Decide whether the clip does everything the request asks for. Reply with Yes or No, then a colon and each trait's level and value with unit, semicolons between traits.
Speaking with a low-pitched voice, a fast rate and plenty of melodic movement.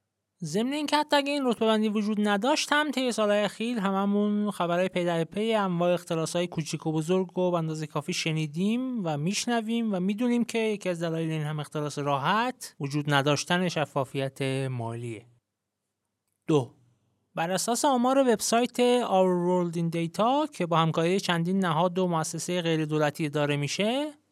No: medium, 180 Hz; fast, 160 wpm; wide, 6.2 semitones